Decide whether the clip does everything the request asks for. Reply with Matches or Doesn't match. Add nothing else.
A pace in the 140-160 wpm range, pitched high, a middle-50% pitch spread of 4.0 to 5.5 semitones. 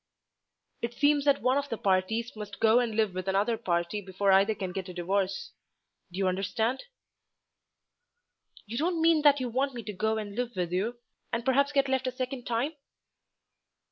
Doesn't match